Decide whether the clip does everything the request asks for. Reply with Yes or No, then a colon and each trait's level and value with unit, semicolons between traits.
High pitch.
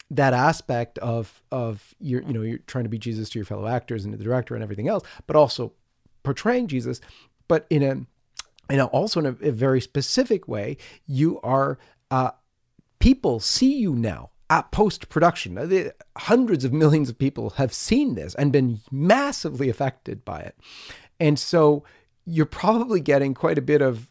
No: low, 135 Hz